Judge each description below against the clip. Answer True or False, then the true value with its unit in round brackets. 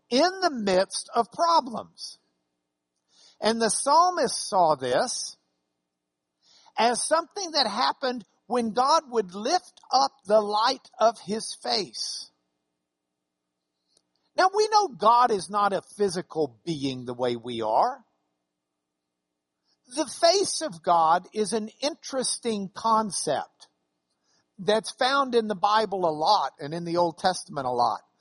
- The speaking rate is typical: False (125 wpm)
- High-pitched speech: True (205 Hz)